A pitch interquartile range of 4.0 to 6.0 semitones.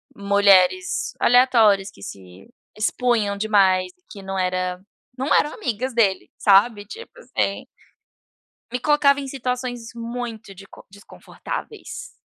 Yes: average, 4.3 semitones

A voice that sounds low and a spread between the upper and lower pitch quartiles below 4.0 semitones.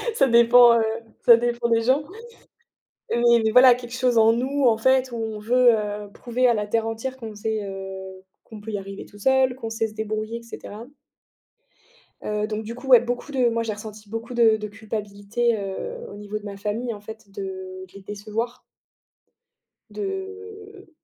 No: high, 225 Hz; average, 2.7 semitones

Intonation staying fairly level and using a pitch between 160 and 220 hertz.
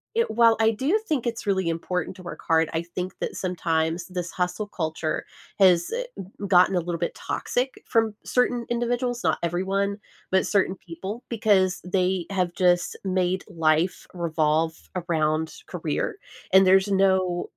No: average, 3.2 semitones; medium, 185 Hz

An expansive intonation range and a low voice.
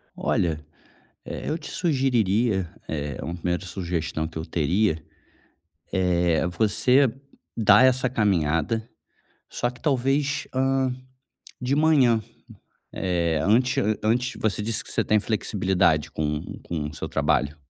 Yes: wide, 6.8 semitones; low, 105 Hz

